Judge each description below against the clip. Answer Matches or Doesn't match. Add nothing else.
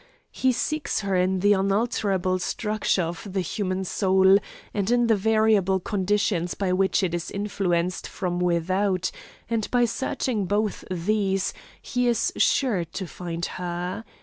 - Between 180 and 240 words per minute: Doesn't match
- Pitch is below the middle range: Doesn't match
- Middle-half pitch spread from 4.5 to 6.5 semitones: Doesn't match